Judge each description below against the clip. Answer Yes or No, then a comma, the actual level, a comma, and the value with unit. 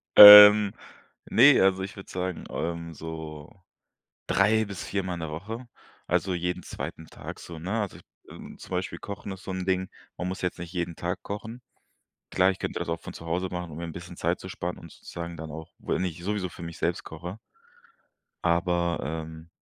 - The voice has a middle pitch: No, very low, 90 Hz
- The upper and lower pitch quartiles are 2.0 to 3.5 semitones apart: Yes, narrow, 2.5 semitones